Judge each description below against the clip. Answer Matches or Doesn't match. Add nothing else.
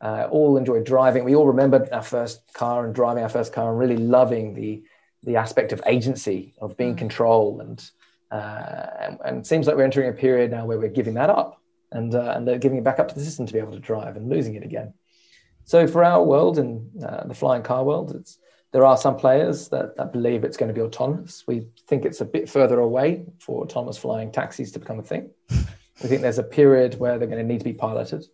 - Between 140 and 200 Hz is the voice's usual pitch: Doesn't match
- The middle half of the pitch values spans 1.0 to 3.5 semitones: Matches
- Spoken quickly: Matches